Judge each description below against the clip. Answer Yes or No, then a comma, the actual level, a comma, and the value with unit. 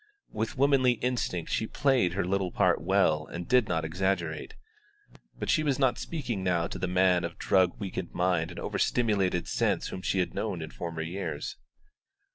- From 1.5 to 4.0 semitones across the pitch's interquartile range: No, average, 4.7 semitones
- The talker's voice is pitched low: Yes, very low, 95 Hz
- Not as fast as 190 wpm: Yes, average, 180 wpm